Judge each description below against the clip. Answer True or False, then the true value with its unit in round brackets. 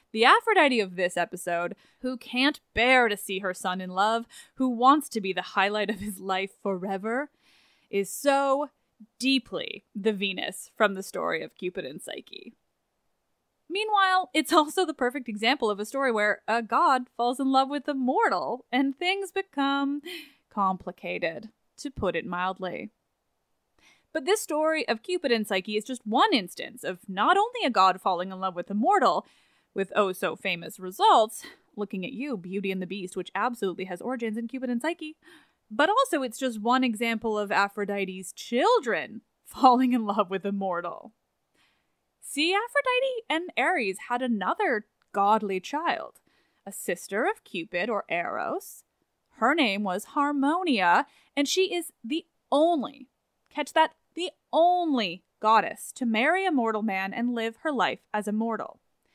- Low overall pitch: False (235 Hz)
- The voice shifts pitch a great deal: True (6.8 semitones)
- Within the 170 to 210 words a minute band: False (160 wpm)